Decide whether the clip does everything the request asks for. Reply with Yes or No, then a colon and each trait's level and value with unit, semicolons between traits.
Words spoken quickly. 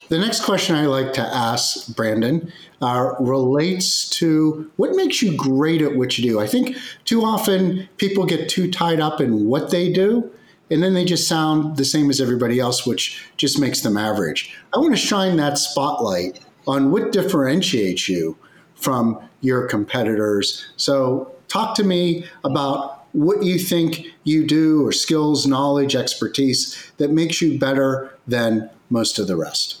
No: average, 165 wpm